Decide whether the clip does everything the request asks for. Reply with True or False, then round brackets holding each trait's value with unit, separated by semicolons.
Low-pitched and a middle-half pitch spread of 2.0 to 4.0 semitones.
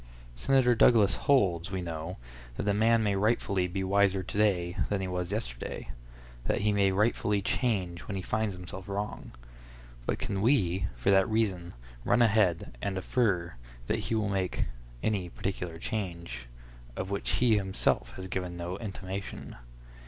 True (95 Hz; 3.1 semitones)